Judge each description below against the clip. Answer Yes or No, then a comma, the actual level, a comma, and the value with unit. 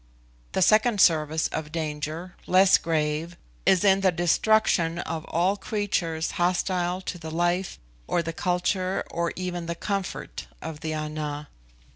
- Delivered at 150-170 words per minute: No, average, 140 wpm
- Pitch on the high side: No, medium, 175 Hz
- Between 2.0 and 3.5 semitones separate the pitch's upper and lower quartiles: Yes, average, 2.7 semitones